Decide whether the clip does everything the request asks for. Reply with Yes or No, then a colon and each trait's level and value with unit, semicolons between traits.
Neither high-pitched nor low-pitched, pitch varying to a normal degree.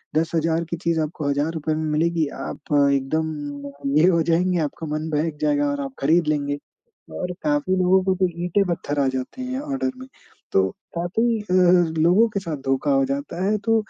Yes: medium, 160 Hz; average, 4.1 semitones